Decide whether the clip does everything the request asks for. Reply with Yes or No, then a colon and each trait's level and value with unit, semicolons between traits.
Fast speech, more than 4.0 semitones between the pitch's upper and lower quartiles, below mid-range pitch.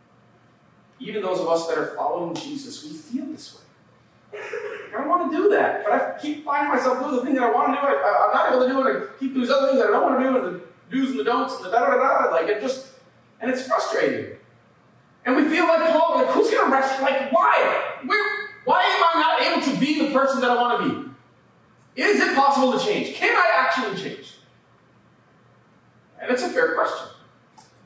No: fast, 225 wpm; average, 4.4 semitones; very high, 275 Hz